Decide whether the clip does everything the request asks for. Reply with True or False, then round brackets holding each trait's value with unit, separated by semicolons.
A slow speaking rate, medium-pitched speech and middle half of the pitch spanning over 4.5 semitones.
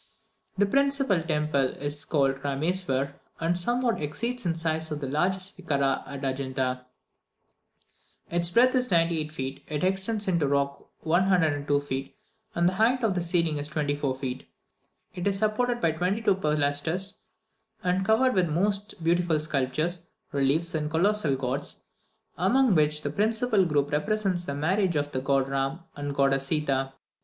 False (160 wpm; 160 Hz; 5.1 semitones)